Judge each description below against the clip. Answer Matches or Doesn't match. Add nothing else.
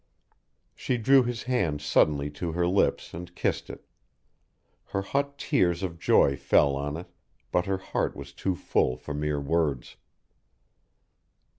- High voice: Doesn't match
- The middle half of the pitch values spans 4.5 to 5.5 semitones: Matches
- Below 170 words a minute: Matches